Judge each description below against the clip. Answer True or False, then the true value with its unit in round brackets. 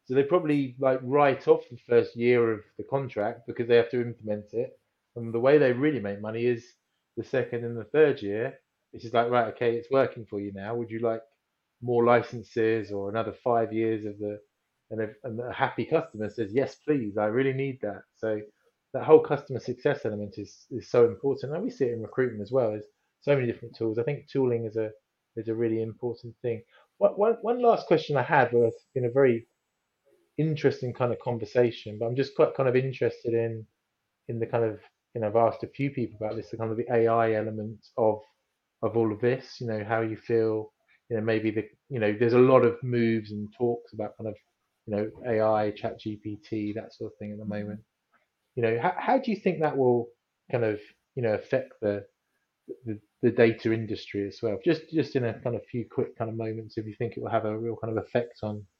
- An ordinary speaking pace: False (225 wpm)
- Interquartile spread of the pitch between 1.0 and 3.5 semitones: True (2.6 semitones)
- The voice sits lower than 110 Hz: False (115 Hz)